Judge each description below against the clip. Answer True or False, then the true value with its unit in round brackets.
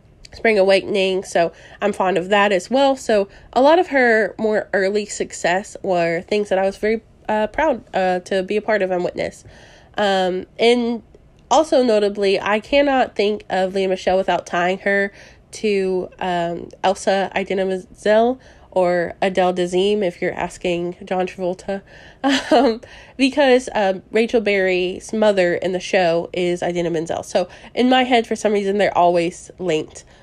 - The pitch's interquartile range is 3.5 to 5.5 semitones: False (3.1 semitones)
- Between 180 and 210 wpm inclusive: False (160 wpm)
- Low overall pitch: False (195 Hz)